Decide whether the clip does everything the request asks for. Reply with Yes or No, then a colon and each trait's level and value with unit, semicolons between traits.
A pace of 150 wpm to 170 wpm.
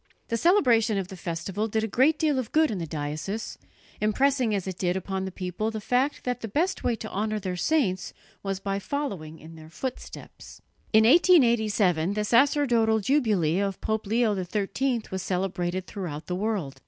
No: average, 180 wpm